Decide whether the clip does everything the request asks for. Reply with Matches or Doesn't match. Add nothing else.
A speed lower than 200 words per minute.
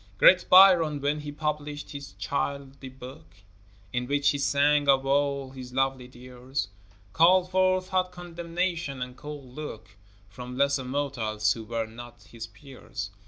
Matches